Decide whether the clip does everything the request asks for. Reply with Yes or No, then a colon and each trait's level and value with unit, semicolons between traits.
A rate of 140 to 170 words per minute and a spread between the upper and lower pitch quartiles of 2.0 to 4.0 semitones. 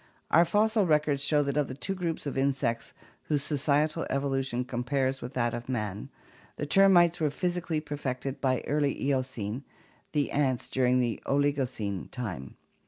Yes: average, 150 wpm; average, 3.0 semitones